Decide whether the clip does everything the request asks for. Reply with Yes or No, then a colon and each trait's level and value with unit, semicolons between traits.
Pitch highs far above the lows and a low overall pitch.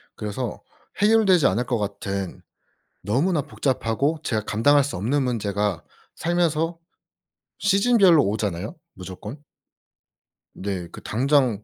Yes: wide, 7.3 semitones; low, 125 Hz